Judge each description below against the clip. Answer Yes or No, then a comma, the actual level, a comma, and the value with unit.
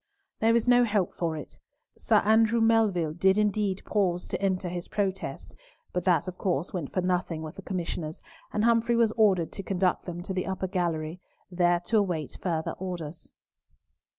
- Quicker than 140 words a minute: Yes, average, 180 wpm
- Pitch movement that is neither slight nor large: Yes, average, 3.2 semitones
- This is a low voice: No, medium, 185 Hz